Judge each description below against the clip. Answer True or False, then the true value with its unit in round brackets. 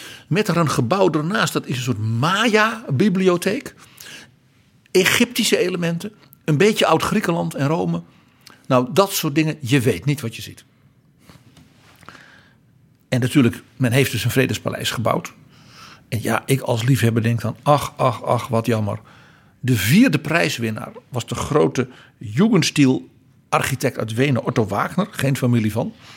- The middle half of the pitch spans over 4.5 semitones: True (5.6 semitones)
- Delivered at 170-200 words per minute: False (140 wpm)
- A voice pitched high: False (135 Hz)